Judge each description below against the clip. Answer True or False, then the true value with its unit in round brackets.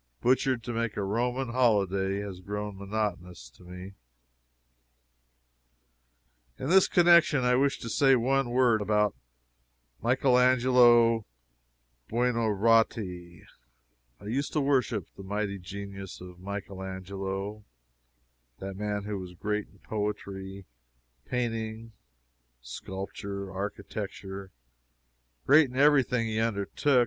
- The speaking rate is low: True (110 wpm)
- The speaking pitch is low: True (105 Hz)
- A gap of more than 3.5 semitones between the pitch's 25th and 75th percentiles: True (4.1 semitones)